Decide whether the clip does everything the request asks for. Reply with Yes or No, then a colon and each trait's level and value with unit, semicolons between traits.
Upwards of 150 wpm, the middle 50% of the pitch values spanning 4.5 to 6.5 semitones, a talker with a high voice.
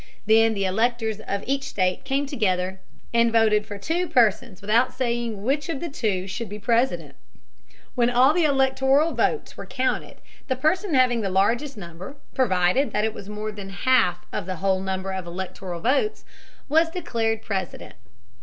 Yes: average, 165 wpm; wide, 5.5 semitones; high, 225 Hz